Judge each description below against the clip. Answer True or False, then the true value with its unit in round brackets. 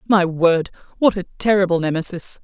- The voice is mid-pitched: True (180 Hz)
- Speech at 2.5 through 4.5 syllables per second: False (5.4 syllables/s)